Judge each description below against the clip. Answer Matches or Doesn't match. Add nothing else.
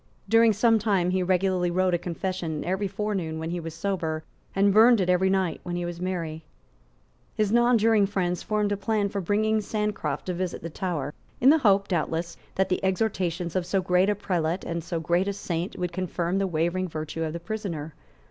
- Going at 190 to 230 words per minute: Matches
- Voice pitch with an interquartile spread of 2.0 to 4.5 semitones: Matches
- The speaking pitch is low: Doesn't match